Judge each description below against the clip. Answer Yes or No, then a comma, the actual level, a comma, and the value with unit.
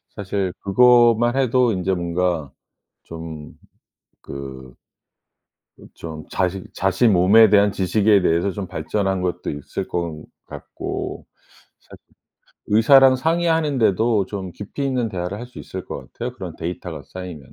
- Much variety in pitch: No, average, 4.8 semitones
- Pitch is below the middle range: Yes, very low, 95 Hz